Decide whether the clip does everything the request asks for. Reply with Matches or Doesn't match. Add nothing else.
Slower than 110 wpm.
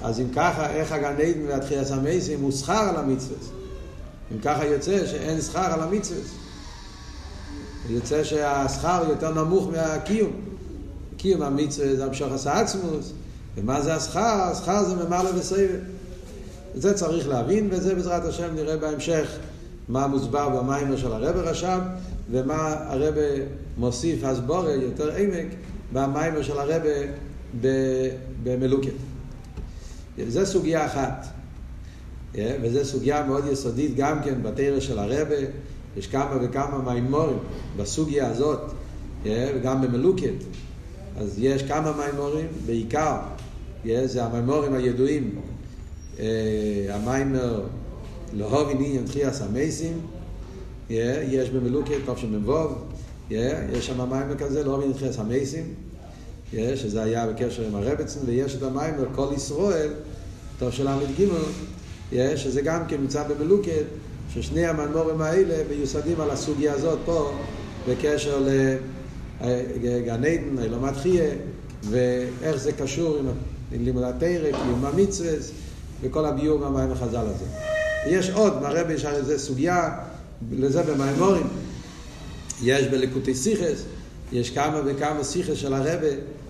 Doesn't match